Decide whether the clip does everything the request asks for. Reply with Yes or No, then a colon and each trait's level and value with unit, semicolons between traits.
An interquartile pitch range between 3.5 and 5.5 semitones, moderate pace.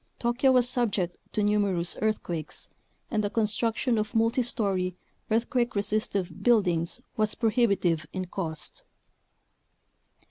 No: average, 4.2 semitones; slow, 115 wpm